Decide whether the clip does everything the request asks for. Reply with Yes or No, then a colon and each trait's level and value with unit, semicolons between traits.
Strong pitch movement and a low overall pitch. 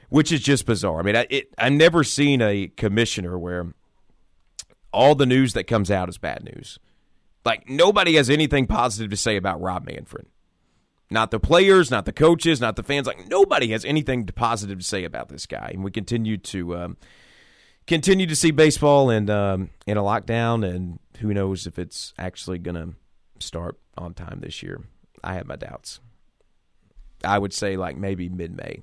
Yes: wide, 6.7 semitones; low, 110 Hz